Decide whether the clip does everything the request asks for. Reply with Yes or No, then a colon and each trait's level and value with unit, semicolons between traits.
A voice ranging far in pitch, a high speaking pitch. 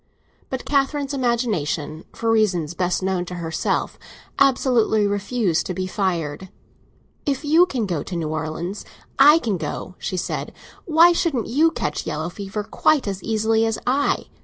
Yes: wide, 6.8 semitones; high, 210 Hz